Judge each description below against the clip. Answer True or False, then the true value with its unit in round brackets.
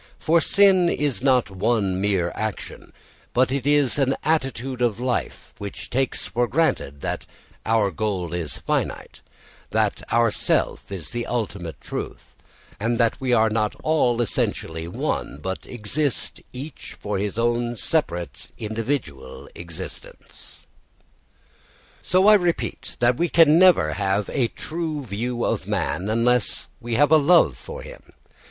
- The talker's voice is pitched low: True (120 Hz)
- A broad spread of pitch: True (6.1 semitones)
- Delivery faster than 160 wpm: False (140 wpm)